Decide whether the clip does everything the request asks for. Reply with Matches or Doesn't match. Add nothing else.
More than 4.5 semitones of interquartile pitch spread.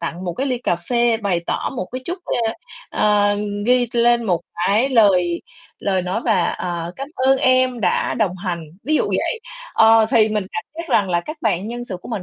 Matches